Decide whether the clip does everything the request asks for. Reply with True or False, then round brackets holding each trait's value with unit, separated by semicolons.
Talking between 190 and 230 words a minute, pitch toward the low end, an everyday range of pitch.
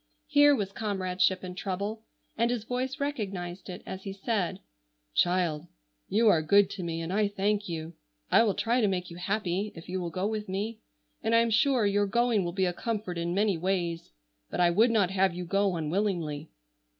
False (200 wpm; 195 Hz; 3.4 semitones)